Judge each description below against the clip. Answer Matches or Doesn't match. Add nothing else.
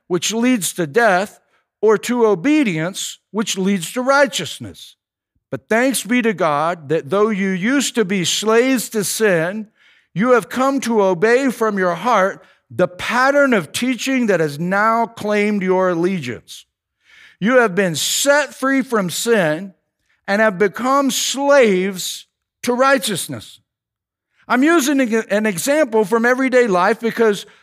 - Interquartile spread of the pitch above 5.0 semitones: Matches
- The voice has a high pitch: Matches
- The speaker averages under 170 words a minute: Matches